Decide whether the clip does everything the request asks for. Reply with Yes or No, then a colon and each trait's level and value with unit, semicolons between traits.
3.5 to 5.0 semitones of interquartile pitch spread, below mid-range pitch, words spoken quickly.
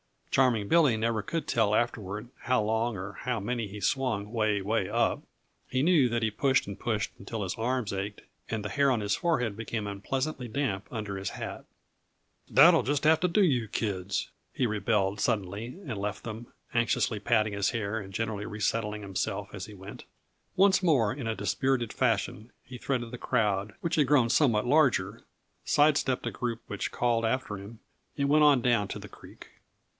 No: average, 3.9 semitones; low, 115 Hz; average, 190 wpm